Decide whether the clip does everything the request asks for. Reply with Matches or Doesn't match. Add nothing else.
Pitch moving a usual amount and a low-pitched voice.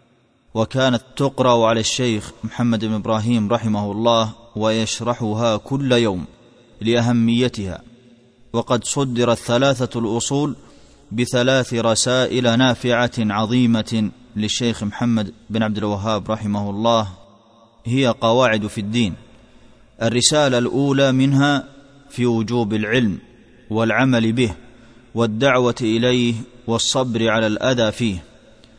Doesn't match